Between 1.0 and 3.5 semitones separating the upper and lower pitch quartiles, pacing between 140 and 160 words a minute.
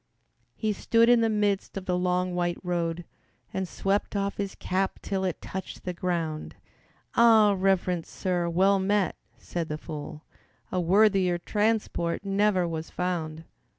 Yes: narrow, 2.6 semitones; average, 150 wpm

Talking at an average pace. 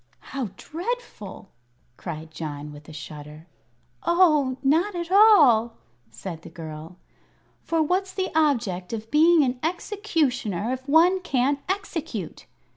No: slow, 120 wpm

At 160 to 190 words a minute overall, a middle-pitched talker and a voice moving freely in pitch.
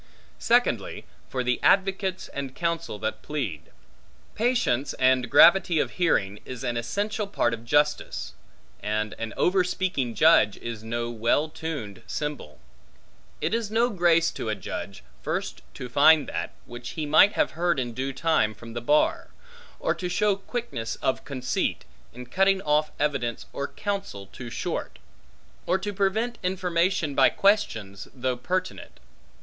No: average, 145 wpm; medium, 145 Hz; wide, 7.7 semitones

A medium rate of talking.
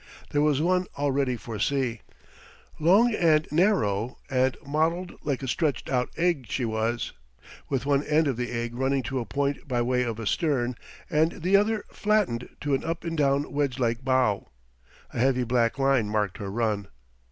Yes: average, 185 wpm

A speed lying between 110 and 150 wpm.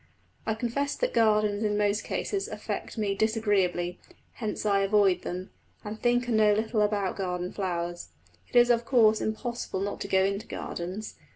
No: average, 170 wpm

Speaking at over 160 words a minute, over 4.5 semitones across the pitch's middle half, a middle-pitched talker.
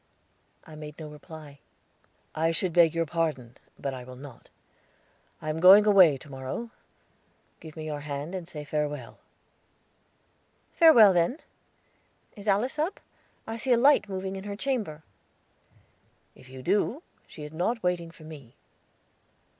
No: average, 145 wpm; average, 5.2 semitones; medium, 165 Hz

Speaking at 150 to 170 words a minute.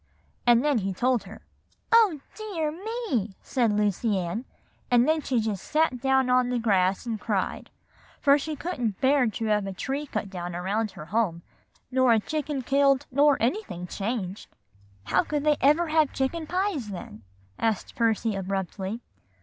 Yes: average, 165 wpm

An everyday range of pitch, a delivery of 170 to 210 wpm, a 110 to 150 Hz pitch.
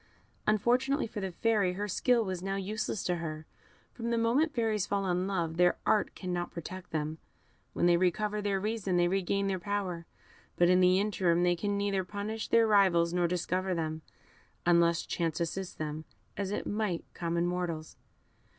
No: average, 3.1 semitones; average, 175 wpm; medium, 185 Hz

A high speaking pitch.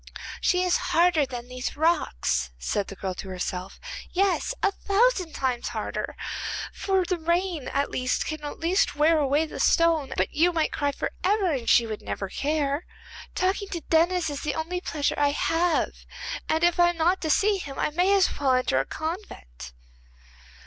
Yes: very high, 315 Hz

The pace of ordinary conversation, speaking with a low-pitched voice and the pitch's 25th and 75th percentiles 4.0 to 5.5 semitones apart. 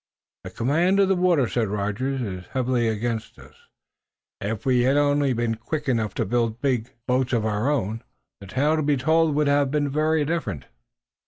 Yes: average, 185 wpm; low, 130 Hz; average, 4.5 semitones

